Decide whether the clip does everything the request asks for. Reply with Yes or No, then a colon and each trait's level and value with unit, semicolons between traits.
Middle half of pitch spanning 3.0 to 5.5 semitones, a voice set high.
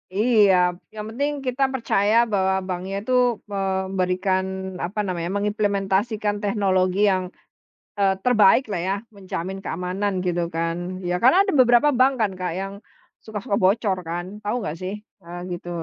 No: narrow, 2.4 semitones; high, 195 Hz